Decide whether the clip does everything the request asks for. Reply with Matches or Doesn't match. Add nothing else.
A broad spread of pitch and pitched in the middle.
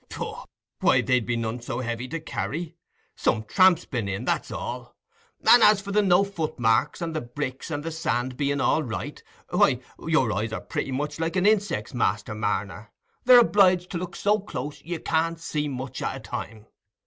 Matches